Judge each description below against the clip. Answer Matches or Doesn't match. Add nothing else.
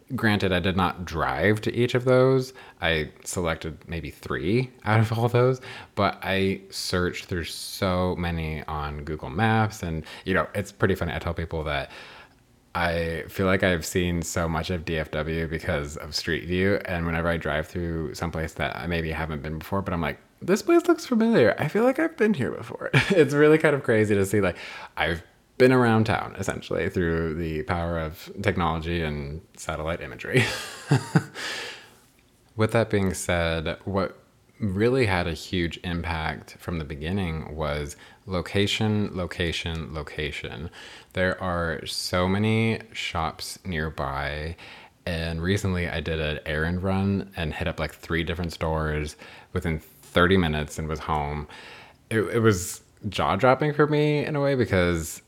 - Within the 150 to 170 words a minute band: Matches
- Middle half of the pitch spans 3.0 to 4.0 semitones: Doesn't match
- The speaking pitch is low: Matches